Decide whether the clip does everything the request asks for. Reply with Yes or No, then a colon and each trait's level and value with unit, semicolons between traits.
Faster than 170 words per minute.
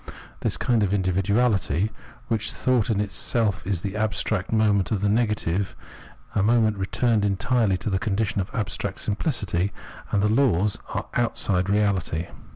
No: average, 160 wpm